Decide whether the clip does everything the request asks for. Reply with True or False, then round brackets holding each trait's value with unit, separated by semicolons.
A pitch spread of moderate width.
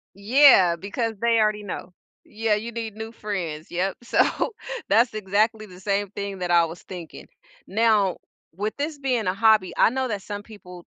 True (3.2 semitones)